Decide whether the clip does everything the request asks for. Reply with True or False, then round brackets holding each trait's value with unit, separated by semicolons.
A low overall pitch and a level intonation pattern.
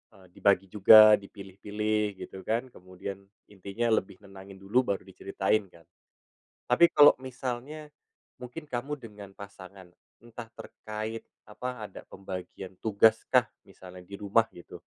False (105 Hz; 3.2 semitones)